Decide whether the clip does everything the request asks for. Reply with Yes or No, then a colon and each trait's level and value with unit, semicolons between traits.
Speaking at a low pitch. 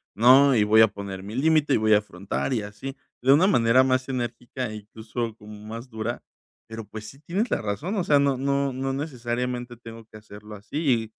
Yes: low, 120 Hz